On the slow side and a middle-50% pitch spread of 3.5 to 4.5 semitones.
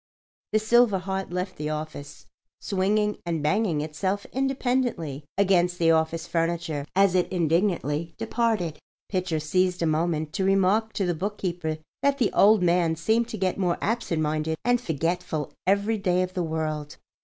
No: average, 155 wpm; average, 4.0 semitones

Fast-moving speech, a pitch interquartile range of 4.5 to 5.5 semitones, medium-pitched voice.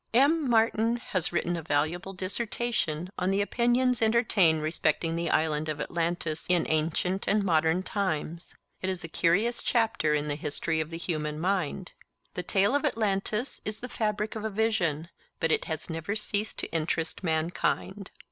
No: average, 165 wpm; average, 5.1 semitones; medium, 180 Hz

